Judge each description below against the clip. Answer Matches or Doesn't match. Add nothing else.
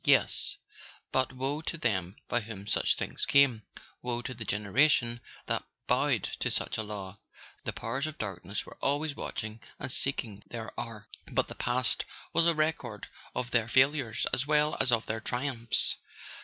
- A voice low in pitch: Matches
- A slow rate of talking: Doesn't match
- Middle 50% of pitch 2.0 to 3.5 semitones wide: Doesn't match